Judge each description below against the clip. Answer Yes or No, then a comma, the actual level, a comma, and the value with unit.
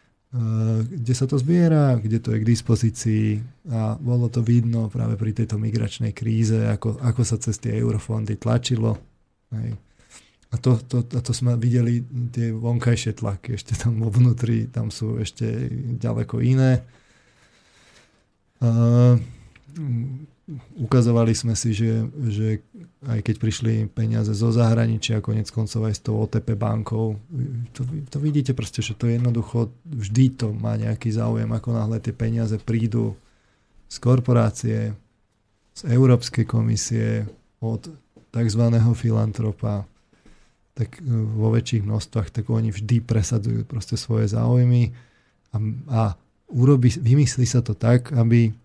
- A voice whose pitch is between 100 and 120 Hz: Yes, low, 115 Hz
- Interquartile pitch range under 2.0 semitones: Yes, narrow, 1.6 semitones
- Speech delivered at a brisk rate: No, average, 130 wpm